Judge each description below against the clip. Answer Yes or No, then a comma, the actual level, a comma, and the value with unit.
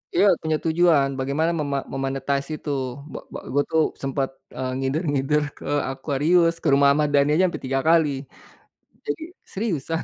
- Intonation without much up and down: No, average, 3.1 semitones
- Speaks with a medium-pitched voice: Yes, medium, 145 Hz